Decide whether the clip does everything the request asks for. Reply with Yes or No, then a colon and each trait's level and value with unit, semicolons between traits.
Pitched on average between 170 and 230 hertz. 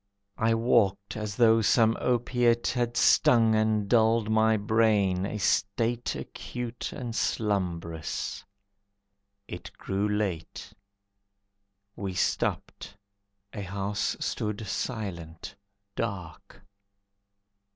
No: low, 105 Hz